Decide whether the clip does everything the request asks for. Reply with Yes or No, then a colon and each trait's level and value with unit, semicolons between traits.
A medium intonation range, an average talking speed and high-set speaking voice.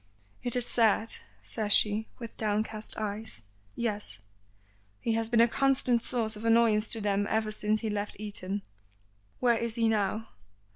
No: narrow, 1.6 semitones; average, 155 wpm; high, 220 Hz